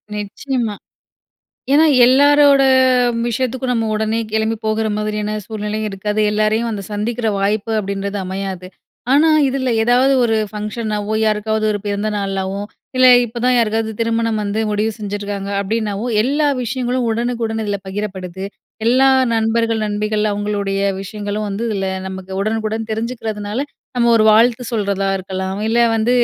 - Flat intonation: Yes, narrow, 2.3 semitones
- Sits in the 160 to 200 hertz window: No, high, 215 Hz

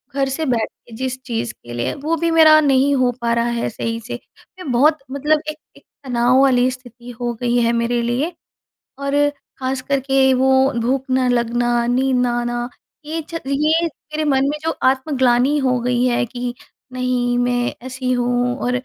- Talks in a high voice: Yes, very high, 255 Hz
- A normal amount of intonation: No, narrow, 2.1 semitones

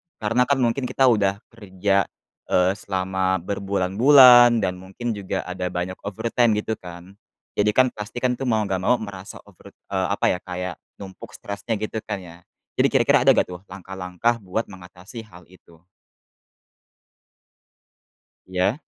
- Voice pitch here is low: Yes, low, 100 Hz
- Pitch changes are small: No, average, 3.7 semitones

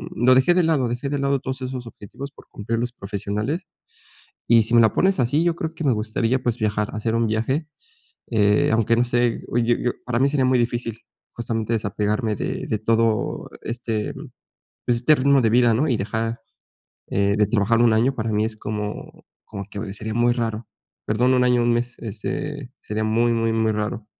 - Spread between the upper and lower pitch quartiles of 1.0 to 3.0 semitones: Yes, narrow, 2.5 semitones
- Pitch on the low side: Yes, low, 115 Hz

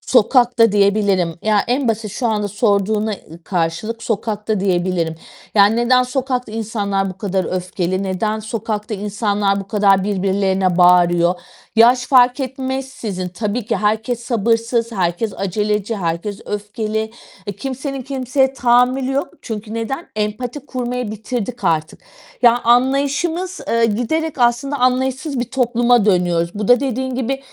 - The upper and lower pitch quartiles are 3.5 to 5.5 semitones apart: Yes, average, 3.9 semitones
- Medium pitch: No, high, 220 Hz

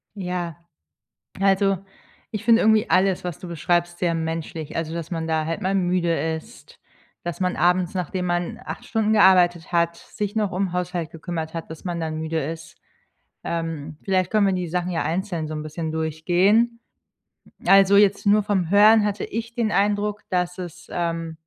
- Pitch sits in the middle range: Yes, medium, 180 Hz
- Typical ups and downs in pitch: Yes, average, 3.2 semitones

